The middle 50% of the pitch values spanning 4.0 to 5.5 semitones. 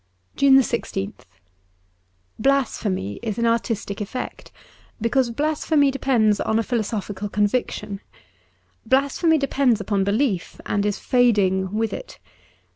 Yes: average, 4.7 semitones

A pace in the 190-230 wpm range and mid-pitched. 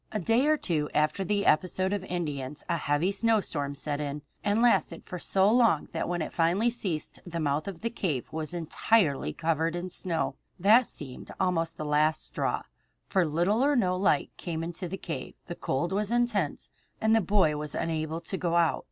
Yes: average, 195 wpm; medium, 175 Hz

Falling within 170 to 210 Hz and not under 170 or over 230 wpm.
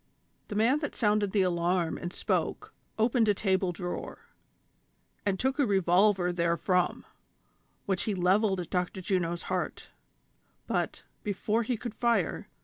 No: high, 190 Hz; average, 140 wpm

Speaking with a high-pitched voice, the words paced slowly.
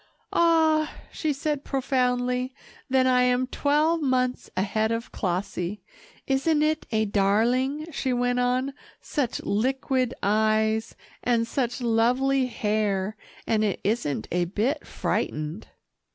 Yes: very high, 250 Hz; slow, 120 wpm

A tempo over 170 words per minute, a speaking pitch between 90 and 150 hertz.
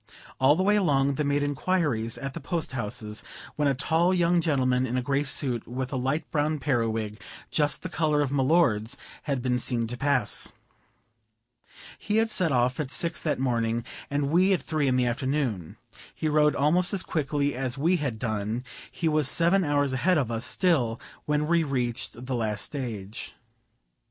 Yes: average, 185 wpm; medium, 140 Hz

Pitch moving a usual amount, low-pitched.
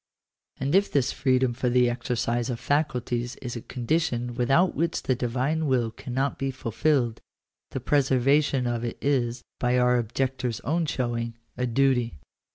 No: narrow, 2.3 semitones; low, 125 Hz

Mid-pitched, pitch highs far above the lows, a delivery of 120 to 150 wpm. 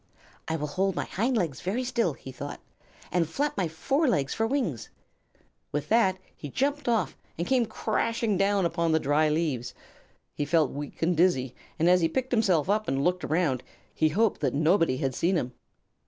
No: medium, 175 Hz; wide, 6.5 semitones; average, 185 wpm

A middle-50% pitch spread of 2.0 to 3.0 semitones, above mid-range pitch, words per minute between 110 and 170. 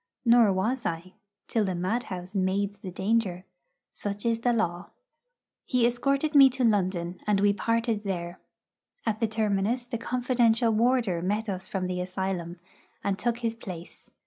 No: average, 3.9 semitones; high, 205 Hz; average, 155 wpm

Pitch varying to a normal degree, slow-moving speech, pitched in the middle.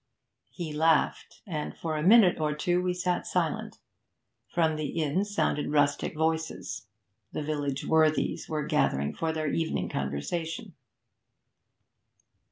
No: narrow, 2.0 semitones; slow, 125 wpm; medium, 155 Hz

